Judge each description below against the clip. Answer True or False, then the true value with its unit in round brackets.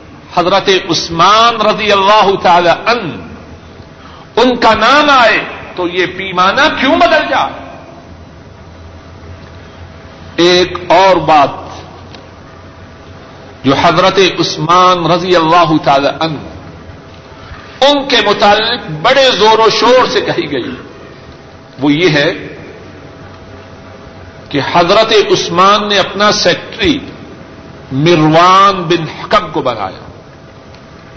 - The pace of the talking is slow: True (95 wpm)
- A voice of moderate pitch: True (175 Hz)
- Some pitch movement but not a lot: False (8.0 semitones)